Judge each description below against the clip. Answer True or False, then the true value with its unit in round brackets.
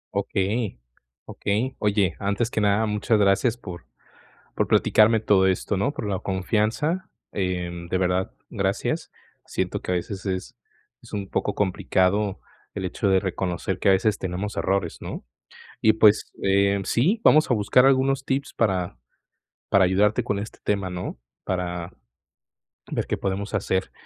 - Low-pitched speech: True (100 Hz)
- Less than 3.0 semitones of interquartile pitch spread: True (2.5 semitones)